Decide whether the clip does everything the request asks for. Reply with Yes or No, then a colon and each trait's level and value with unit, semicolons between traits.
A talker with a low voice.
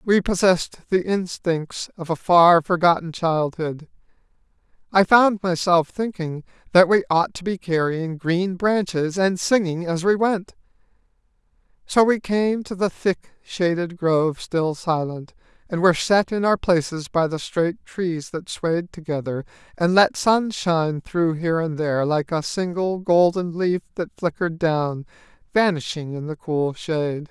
No: medium, 175 Hz